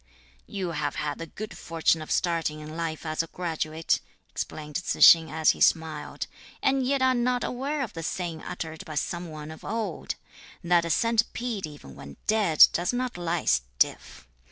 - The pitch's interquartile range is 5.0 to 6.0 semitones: Yes, wide, 5.5 semitones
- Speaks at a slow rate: No, average, 180 wpm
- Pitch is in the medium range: Yes, medium, 165 Hz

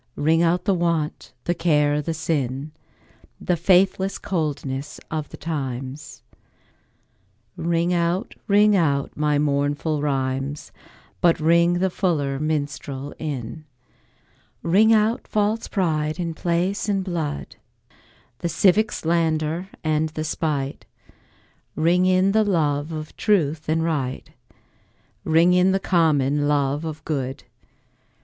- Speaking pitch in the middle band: Yes, medium, 160 Hz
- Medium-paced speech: No, slow, 120 wpm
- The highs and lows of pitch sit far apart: No, average, 3.4 semitones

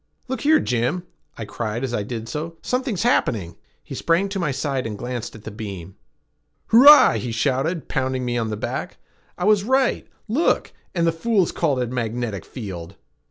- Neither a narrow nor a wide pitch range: No, wide, 8.3 semitones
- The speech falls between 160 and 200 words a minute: Yes, average, 185 wpm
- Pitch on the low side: Yes, low, 130 Hz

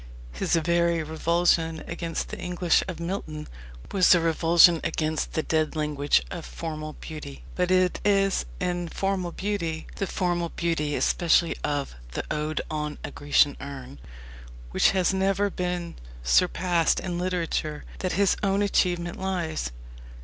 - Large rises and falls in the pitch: No, average, 2.7 semitones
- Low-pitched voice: No, medium, 170 Hz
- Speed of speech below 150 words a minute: Yes, average, 140 wpm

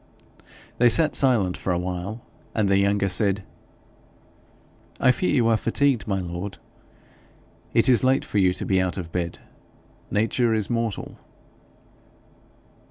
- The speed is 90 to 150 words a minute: Yes, average, 140 wpm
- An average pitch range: Yes, average, 4.0 semitones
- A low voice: Yes, low, 100 Hz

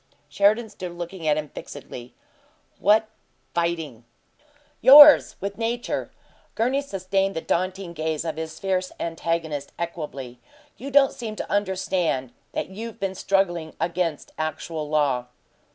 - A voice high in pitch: No, medium, 175 Hz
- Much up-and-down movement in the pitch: No, average, 4.1 semitones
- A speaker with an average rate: No, slow, 125 wpm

